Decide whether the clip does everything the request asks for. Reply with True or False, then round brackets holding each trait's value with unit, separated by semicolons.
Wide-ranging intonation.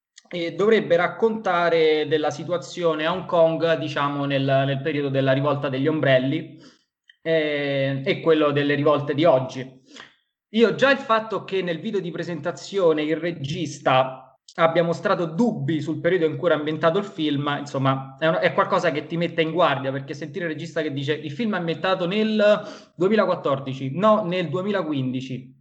False (3.4 semitones)